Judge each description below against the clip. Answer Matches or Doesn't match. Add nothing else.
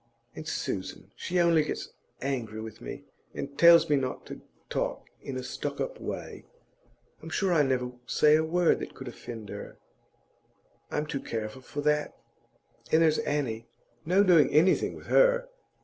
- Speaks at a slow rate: Doesn't match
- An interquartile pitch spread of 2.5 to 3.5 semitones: Doesn't match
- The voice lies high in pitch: Doesn't match